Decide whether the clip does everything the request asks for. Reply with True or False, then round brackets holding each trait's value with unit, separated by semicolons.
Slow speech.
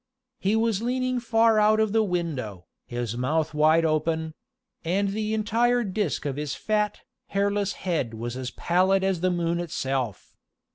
False (155 wpm)